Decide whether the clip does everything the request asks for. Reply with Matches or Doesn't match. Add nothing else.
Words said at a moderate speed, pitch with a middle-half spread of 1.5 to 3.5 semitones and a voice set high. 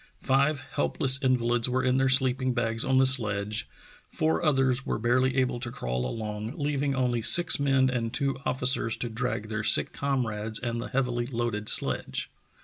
Doesn't match